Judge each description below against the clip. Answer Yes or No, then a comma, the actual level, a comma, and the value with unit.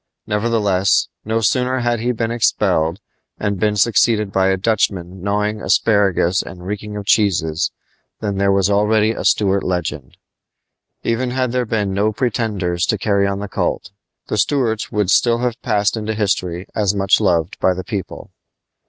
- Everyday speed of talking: Yes, average, 160 wpm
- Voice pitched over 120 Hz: No, low, 105 Hz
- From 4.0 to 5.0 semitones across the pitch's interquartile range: No, narrow, 2.6 semitones